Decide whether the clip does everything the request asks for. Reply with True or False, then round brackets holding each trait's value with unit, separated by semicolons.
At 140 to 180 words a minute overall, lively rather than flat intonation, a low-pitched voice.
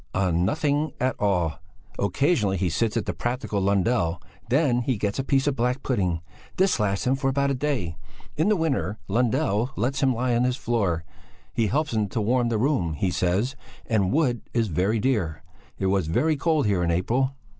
False (195 wpm; 5.8 semitones; 115 Hz)